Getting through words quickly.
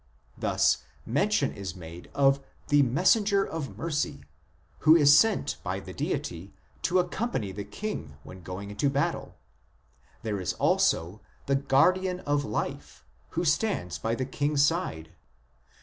No: average, 155 wpm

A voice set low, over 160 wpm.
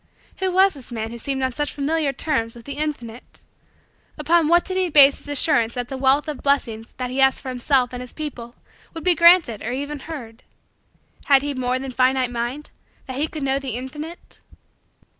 No: very high, 270 Hz; average, 195 wpm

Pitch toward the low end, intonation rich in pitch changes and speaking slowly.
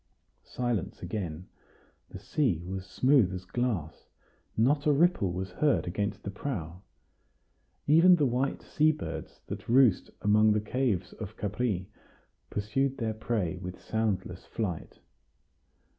Yes: low, 105 Hz; wide, 5.8 semitones; slow, 130 wpm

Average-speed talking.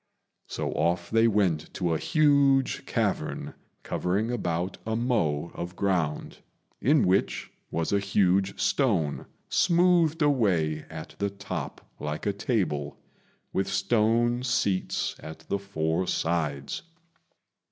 No: slow, 120 wpm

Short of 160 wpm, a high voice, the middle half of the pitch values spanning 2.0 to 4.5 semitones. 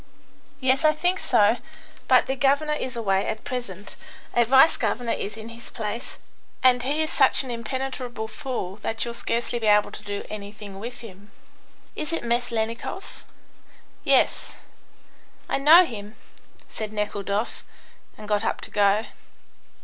Yes: average, 150 wpm; high, 230 Hz; average, 3.8 semitones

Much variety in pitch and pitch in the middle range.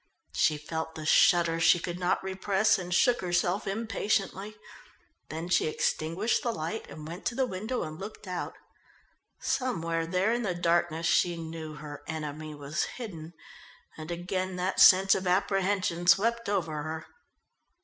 No: average, 3.3 semitones; medium, 175 Hz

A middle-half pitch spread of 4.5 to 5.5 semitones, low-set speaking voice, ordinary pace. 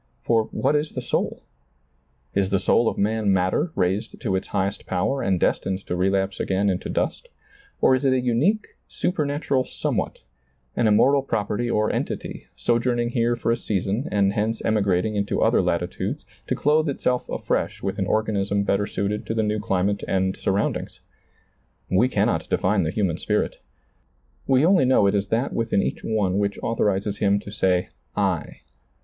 No: average, 3.6 semitones; low, 105 Hz; average, 170 wpm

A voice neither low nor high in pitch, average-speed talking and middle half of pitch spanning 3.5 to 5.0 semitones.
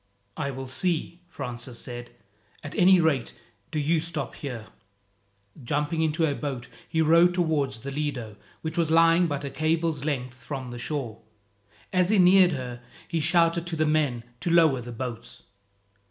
Yes: medium, 150 Hz; average, 165 wpm; average, 4.4 semitones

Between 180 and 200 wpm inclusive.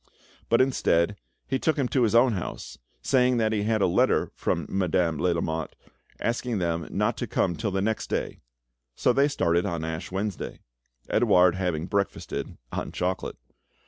No: average, 170 wpm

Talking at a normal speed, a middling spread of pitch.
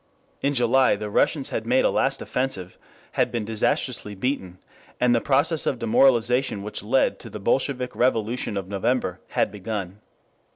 Yes: average, 160 wpm; average, 3.8 semitones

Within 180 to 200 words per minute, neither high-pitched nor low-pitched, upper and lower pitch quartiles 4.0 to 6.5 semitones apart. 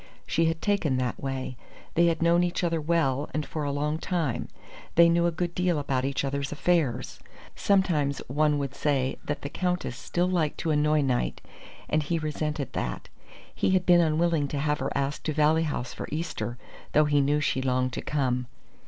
No: average, 195 wpm; medium, 150 Hz; average, 3.3 semitones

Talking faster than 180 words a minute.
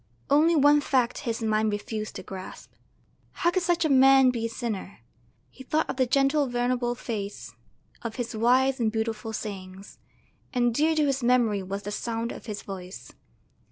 No: average, 175 wpm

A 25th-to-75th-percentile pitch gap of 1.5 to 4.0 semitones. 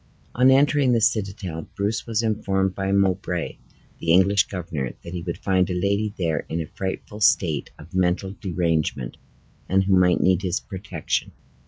Yes: average, 2.7 semitones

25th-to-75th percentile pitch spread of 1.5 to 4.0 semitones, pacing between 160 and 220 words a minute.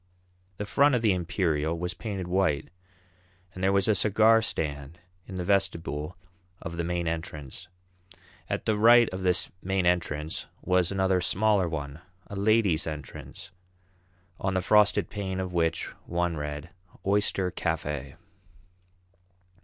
No: average, 3.3 semitones; average, 140 wpm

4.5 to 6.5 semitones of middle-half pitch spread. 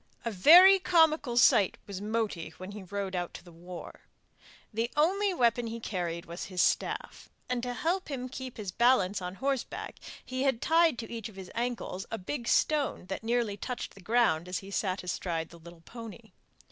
Yes: wide, 5.6 semitones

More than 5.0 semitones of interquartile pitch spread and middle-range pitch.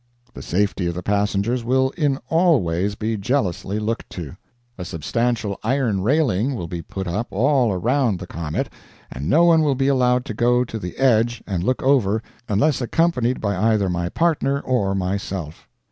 No: wide, 5.4 semitones; low, 110 Hz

